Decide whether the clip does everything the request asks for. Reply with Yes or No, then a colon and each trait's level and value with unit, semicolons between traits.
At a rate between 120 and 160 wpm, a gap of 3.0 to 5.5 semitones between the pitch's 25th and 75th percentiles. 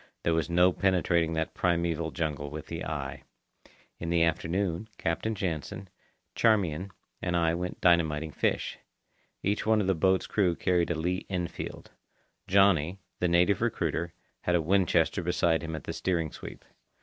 No: average, 155 wpm; narrow, 2.4 semitones